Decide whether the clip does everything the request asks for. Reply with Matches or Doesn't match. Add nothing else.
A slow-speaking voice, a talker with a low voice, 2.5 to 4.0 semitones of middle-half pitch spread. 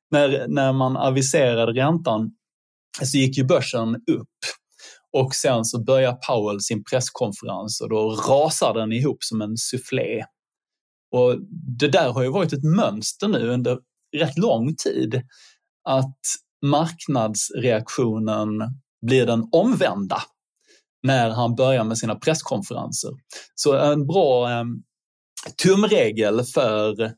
Matches